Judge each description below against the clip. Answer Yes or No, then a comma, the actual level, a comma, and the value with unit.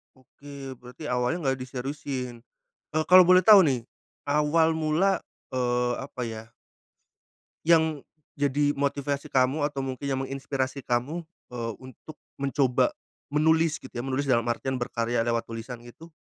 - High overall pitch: No, low, 135 Hz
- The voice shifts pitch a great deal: No, average, 3.3 semitones